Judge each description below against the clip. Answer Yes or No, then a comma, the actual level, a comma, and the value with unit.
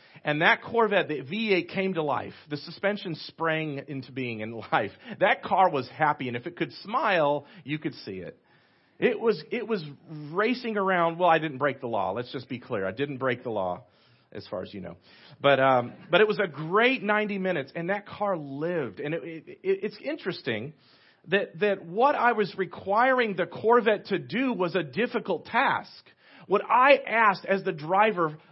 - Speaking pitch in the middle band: Yes, medium, 170 Hz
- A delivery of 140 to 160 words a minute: No, average, 195 wpm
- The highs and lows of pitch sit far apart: Yes, wide, 5.9 semitones